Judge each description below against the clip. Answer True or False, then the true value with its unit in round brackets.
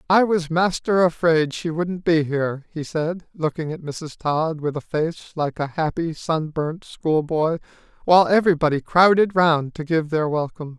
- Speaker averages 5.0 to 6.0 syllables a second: False (4.6 syllables/s)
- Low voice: False (160 Hz)